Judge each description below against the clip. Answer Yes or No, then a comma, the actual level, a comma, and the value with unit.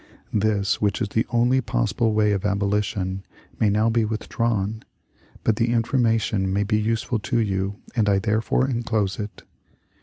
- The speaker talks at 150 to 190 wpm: Yes, average, 155 wpm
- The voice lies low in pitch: Yes, low, 110 Hz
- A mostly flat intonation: Yes, narrow, 2.2 semitones